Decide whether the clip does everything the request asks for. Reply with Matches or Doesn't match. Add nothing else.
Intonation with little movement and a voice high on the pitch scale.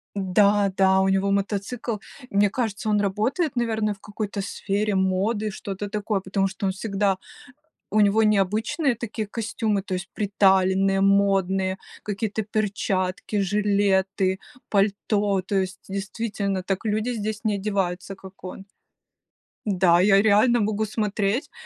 Matches